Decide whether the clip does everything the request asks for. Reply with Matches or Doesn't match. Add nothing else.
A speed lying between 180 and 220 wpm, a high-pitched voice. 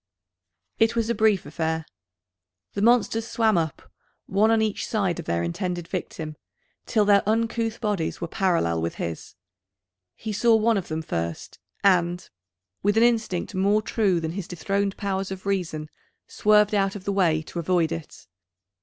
Doesn't match